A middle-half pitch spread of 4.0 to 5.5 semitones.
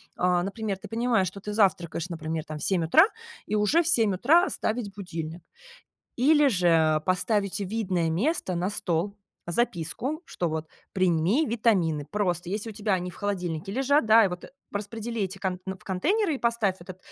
Yes: average, 4.4 semitones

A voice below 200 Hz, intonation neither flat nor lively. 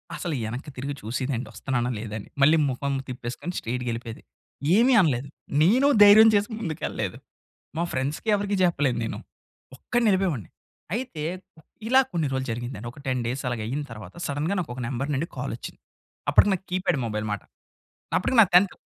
No: medium, 140 Hz; wide, 7.2 semitones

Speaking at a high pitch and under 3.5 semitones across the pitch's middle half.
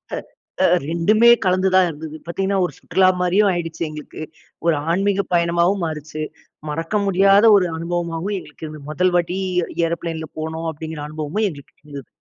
No: medium, 170 Hz; average, 3.0 semitones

